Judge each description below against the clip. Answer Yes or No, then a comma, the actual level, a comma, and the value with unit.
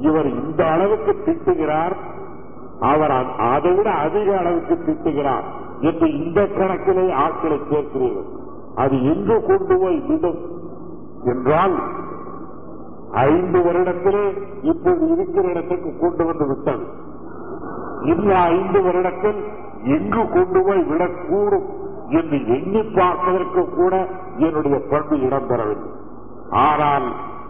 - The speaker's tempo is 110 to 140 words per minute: No, average, 95 wpm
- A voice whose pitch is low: No, high, 200 Hz